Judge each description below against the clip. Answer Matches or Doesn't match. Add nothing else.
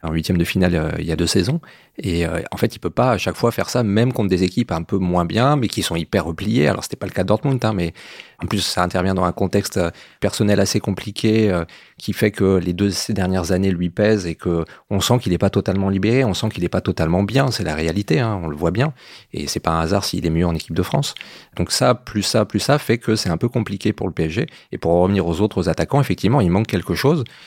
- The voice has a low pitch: Matches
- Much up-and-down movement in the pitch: Doesn't match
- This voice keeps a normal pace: Doesn't match